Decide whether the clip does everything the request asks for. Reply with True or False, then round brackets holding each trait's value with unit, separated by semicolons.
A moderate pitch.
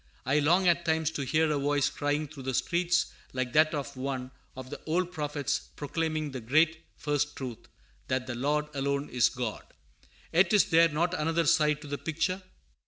True (150 Hz)